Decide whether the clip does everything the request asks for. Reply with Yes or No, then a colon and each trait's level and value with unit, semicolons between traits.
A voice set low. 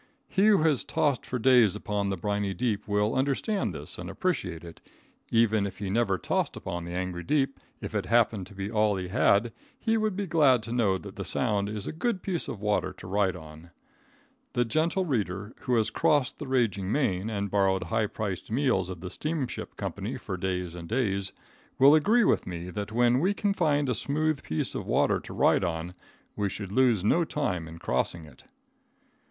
Yes: low, 105 Hz